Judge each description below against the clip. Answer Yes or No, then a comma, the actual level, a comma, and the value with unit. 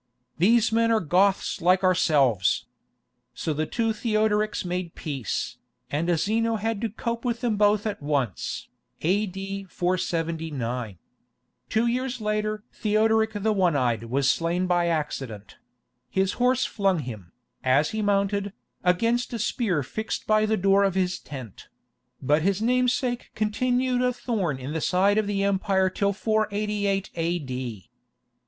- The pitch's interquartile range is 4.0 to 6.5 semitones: Yes, average, 5.1 semitones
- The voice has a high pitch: Yes, high, 195 Hz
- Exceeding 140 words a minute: No, slow, 135 wpm